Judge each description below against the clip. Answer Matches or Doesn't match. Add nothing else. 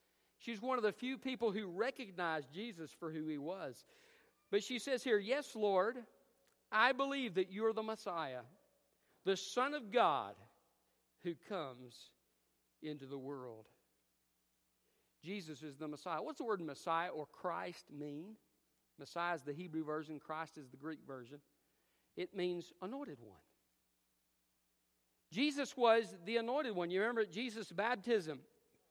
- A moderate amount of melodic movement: Doesn't match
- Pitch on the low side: Doesn't match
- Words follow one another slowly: Doesn't match